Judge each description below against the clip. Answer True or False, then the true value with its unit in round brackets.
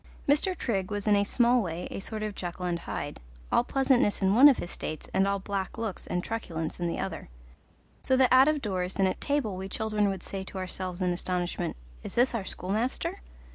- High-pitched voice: True (200 Hz)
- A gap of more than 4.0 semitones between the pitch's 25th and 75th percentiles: True (4.4 semitones)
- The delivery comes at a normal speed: False (215 wpm)